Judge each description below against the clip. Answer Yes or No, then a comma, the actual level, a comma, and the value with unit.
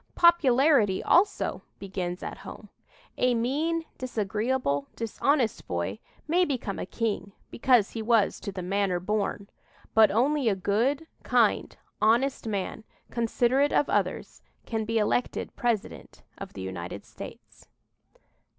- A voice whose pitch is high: Yes, high, 225 Hz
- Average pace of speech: No, slow, 125 wpm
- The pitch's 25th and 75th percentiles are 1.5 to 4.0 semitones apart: No, average, 4.8 semitones